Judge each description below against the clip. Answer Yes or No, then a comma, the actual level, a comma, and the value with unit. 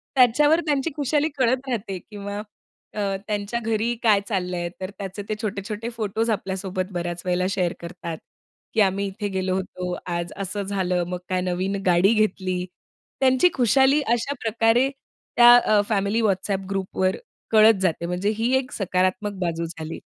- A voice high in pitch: Yes, high, 200 Hz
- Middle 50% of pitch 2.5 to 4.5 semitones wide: Yes, average, 3.7 semitones